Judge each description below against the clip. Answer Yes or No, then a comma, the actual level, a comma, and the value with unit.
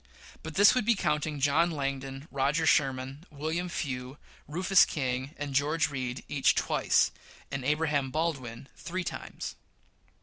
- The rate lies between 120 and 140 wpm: Yes, slow, 135 wpm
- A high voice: No, medium, 145 Hz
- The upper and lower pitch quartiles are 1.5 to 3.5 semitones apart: Yes, average, 3.2 semitones